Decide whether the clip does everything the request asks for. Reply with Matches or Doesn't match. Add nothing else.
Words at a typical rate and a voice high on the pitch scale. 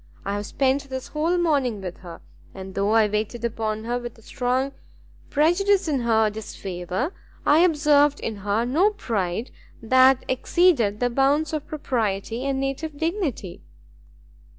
Matches